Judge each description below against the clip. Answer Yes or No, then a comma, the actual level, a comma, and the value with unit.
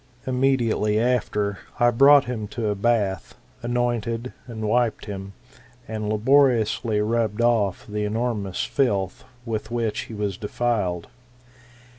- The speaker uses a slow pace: Yes, slow, 125 wpm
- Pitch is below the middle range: Yes, low, 110 Hz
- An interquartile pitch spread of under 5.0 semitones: Yes, narrow, 2.5 semitones